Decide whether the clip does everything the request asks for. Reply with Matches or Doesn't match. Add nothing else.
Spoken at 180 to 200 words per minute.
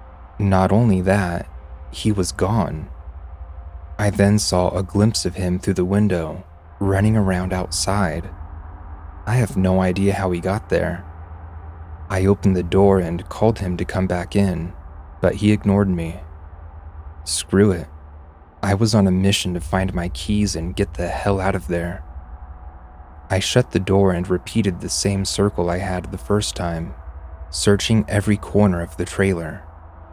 Doesn't match